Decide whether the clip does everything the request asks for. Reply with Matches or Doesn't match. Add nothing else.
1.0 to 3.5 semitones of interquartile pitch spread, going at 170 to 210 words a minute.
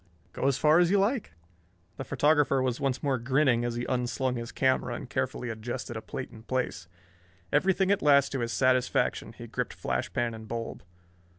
Matches